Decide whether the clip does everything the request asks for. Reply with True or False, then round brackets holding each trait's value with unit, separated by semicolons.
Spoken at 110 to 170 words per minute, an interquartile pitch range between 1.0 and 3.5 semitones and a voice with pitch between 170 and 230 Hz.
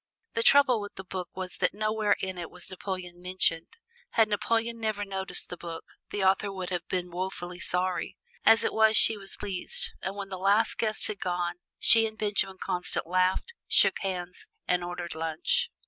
False (185 wpm; 2.8 semitones; 190 Hz)